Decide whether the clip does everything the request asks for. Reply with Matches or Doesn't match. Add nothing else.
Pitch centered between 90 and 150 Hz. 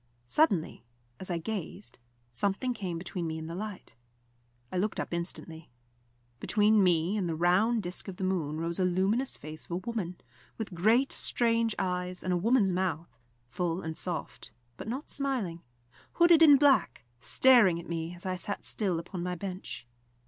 Doesn't match